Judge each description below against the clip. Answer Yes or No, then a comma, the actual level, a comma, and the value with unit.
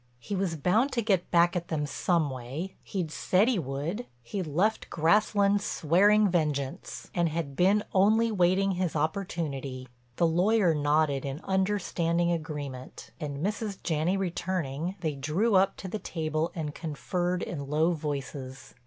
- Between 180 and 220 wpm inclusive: No, average, 145 wpm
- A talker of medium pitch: Yes, medium, 170 Hz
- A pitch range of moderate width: Yes, average, 4.5 semitones